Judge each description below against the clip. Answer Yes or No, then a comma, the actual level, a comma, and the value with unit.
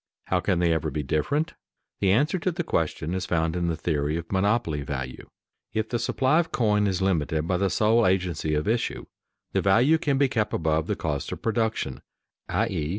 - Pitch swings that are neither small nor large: No, wide, 6.2 semitones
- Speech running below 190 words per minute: No, average, 200 wpm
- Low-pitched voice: Yes, very low, 95 Hz